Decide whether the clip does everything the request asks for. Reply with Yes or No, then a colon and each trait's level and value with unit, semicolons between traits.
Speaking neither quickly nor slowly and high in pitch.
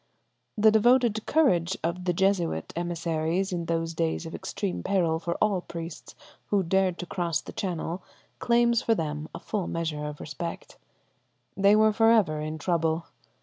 No: average, 160 wpm; medium, 175 Hz